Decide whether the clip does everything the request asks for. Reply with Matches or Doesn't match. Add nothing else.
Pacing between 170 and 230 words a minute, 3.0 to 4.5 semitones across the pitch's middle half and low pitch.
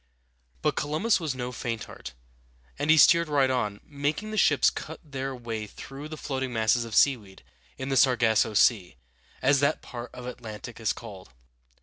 Matches